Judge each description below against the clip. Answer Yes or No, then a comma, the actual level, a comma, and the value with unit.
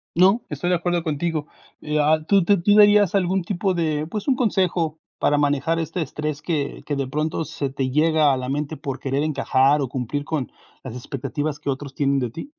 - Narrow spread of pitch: No, average, 3.6 semitones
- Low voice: No, medium, 150 Hz